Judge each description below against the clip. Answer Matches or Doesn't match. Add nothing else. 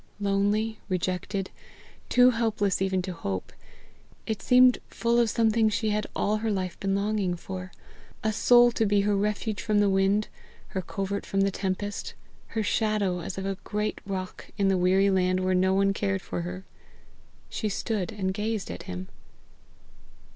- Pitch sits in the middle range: Doesn't match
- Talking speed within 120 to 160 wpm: Doesn't match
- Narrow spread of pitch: Matches